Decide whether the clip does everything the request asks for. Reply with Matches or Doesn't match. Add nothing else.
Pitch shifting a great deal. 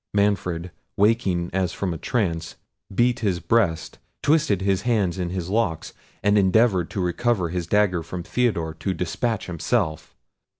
Doesn't match